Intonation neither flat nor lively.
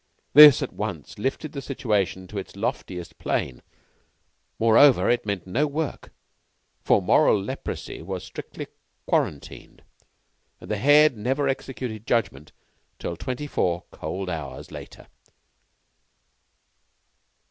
No: wide, 6.8 semitones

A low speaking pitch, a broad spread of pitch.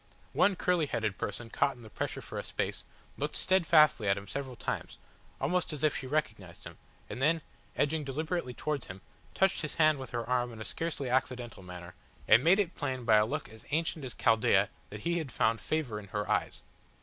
Yes: low, 130 Hz; wide, 5.9 semitones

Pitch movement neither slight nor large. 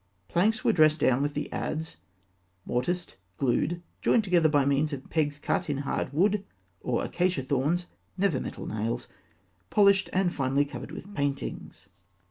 Yes: average, 4.4 semitones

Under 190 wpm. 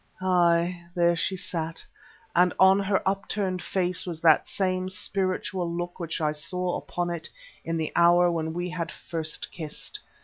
Yes: average, 160 wpm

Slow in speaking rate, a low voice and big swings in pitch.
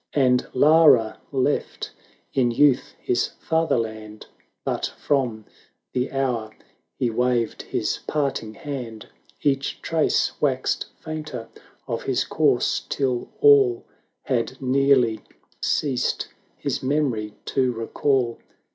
No: slow, 105 wpm; low, 130 Hz; average, 3.3 semitones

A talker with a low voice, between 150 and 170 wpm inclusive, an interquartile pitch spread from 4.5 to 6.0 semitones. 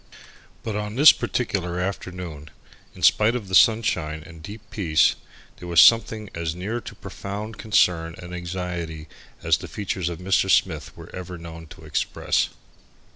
No: very low, 90 Hz; average, 155 wpm; average, 3.9 semitones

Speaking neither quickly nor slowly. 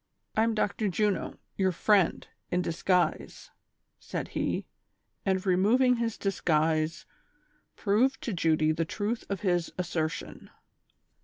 No: slow, 120 wpm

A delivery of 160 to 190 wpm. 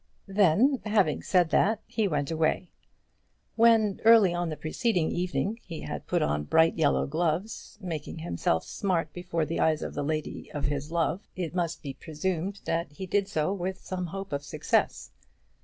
Yes: average, 175 wpm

